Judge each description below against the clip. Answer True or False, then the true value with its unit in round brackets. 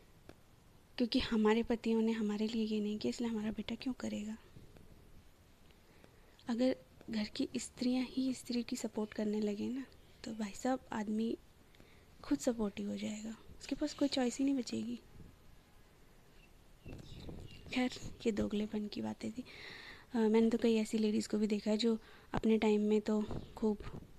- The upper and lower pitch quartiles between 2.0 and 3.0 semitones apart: True (2.6 semitones)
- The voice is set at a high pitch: True (225 Hz)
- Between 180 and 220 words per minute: False (155 wpm)